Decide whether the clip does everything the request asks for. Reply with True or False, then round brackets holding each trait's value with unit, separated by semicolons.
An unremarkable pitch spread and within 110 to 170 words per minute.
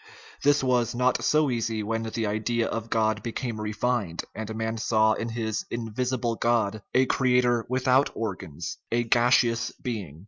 False (2.1 semitones; 160 wpm)